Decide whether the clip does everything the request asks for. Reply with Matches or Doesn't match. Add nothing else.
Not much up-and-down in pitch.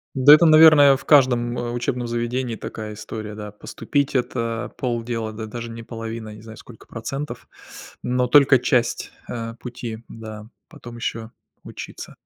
Matches